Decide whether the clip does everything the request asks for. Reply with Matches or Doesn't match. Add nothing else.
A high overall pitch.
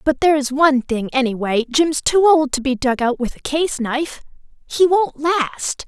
Matches